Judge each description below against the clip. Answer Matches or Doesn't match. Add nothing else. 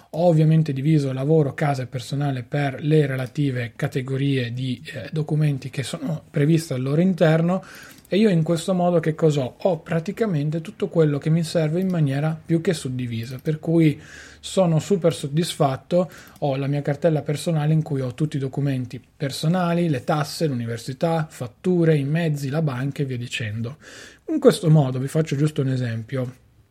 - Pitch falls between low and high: Matches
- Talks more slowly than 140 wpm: Doesn't match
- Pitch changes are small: Doesn't match